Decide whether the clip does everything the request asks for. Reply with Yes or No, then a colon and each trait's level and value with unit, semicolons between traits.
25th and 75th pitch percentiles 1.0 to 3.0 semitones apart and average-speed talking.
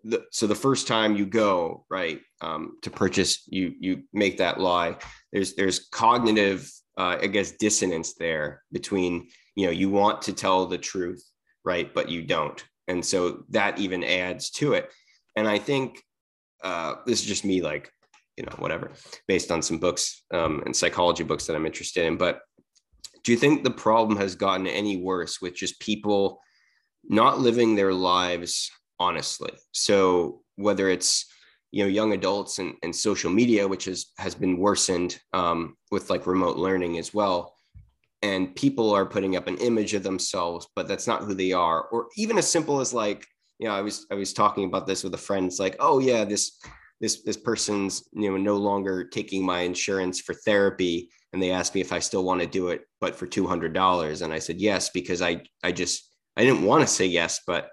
Yes: narrow, 2.6 semitones; average, 195 wpm